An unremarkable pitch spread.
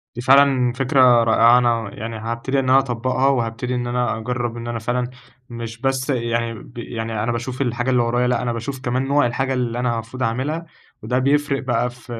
No: narrow, 1.9 semitones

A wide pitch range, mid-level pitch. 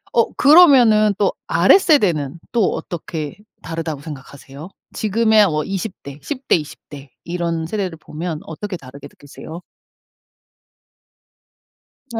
Yes: wide, 5.9 semitones; medium, 170 Hz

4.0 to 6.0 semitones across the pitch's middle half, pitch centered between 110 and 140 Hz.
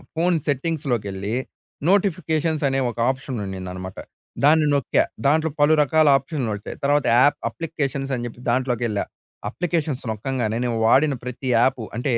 Yes: average, 4.8 semitones; low, 135 Hz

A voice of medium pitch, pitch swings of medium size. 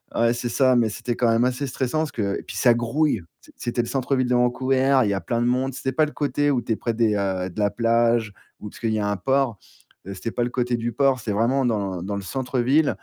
No: low, 120 Hz; average, 3.1 semitones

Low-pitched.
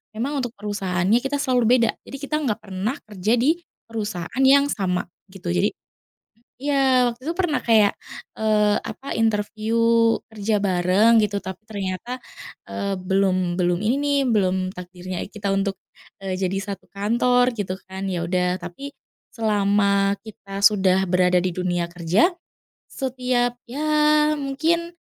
No: high, 210 Hz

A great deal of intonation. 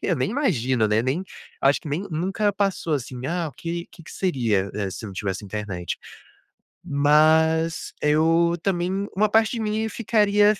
Yes: wide, 7.3 semitones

